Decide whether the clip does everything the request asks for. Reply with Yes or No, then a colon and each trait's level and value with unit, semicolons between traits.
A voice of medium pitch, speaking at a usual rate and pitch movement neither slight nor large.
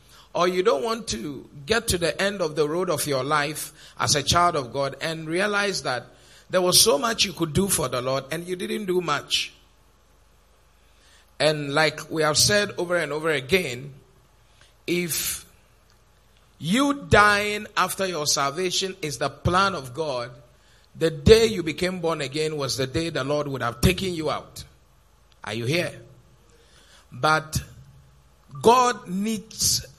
No: medium, 150 Hz; average, 160 wpm; wide, 6.8 semitones